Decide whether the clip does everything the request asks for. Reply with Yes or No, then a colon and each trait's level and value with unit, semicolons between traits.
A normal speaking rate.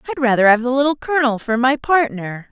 No: fast, 215 wpm